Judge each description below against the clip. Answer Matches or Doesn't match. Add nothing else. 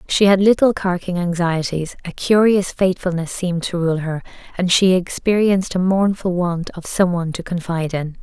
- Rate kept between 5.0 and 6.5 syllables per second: Matches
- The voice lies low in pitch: Doesn't match